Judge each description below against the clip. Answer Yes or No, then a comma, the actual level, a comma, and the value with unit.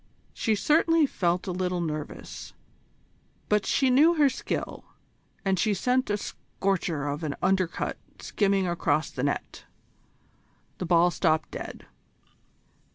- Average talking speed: No, slow, 125 wpm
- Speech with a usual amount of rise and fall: Yes, average, 4.6 semitones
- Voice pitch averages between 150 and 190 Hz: Yes, medium, 185 Hz